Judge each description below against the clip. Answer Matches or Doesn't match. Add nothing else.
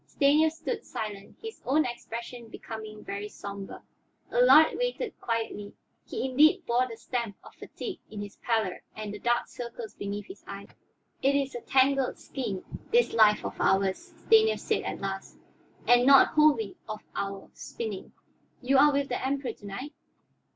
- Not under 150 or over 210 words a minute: Matches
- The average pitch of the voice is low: Doesn't match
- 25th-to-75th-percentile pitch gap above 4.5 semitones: Matches